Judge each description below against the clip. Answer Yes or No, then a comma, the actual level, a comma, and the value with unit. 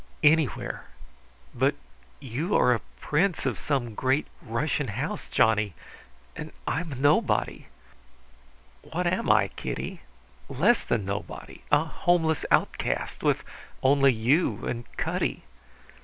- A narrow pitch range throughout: No, average, 5.3 semitones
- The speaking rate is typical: No, slow, 115 wpm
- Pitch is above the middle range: No, medium, 140 Hz